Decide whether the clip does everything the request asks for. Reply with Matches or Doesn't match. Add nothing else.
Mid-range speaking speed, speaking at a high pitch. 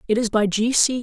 Doesn't match